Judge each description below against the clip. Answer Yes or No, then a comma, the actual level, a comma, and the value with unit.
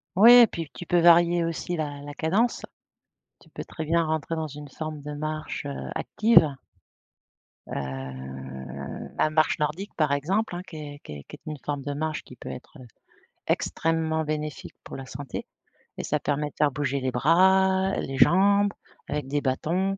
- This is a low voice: No, medium, 155 Hz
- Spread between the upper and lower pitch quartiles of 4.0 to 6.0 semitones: No, average, 3.3 semitones